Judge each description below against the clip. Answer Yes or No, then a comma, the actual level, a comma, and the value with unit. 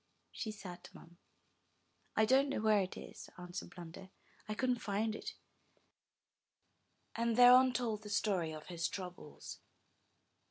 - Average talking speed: No, slow, 130 wpm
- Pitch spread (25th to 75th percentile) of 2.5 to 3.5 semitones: No, average, 4.7 semitones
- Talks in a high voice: Yes, high, 210 Hz